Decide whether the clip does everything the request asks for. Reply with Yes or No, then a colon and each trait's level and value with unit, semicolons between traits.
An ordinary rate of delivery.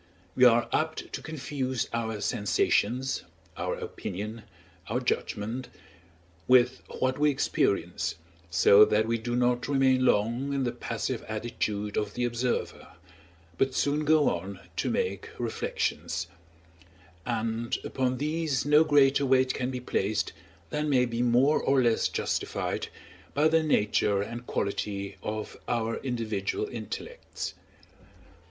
No: slow, 130 wpm